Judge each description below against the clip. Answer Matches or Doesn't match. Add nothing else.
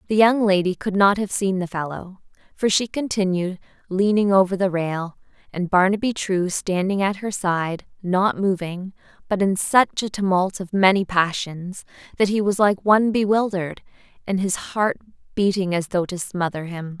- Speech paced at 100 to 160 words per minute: Doesn't match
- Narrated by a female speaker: Matches